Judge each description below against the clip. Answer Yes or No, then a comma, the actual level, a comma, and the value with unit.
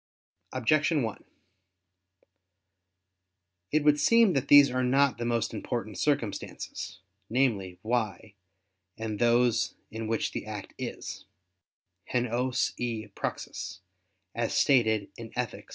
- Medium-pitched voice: No, low, 120 Hz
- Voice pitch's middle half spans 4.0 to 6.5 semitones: No, average, 3.1 semitones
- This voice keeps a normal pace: No, slow, 115 wpm